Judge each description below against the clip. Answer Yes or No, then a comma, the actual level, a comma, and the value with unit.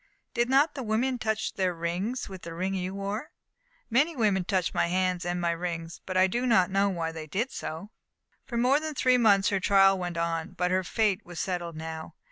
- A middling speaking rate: No, fast, 215 wpm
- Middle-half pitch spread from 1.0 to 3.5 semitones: No, average, 4.4 semitones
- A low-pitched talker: No, high, 190 Hz